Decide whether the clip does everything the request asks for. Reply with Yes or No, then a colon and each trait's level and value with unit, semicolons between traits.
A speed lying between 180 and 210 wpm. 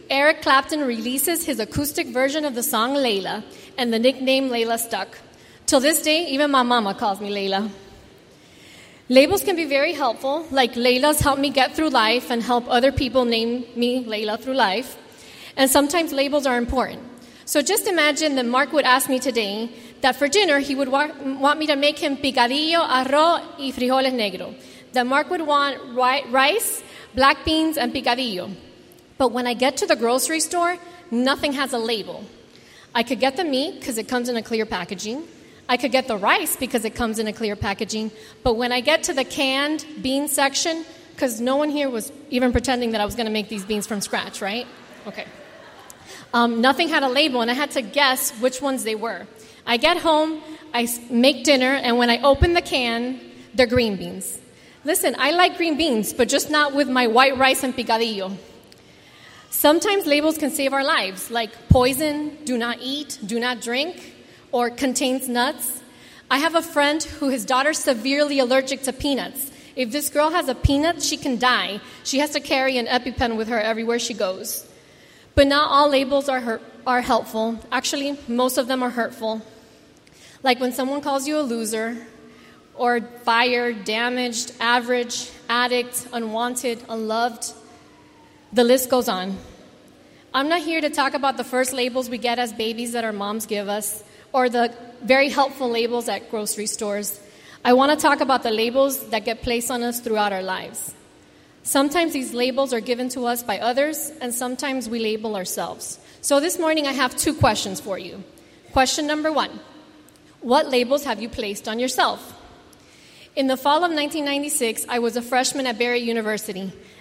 Yes: average, 185 wpm